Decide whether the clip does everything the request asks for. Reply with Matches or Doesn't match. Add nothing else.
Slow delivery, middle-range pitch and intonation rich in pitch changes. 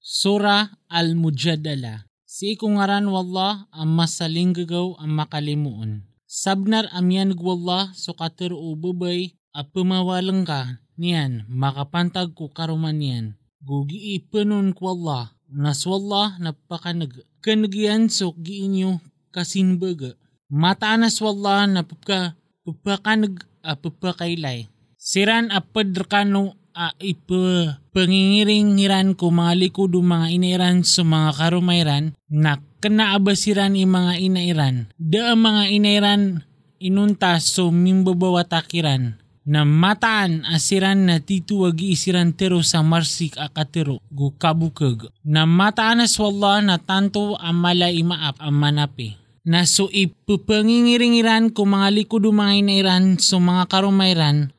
Doesn't match